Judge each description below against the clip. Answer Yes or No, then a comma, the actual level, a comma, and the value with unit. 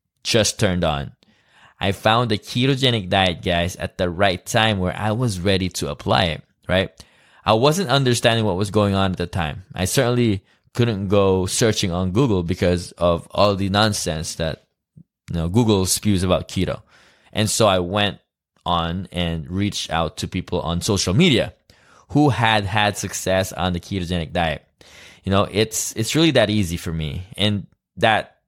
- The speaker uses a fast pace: No, average, 175 wpm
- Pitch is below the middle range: Yes, low, 100 Hz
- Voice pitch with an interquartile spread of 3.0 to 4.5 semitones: Yes, average, 3.5 semitones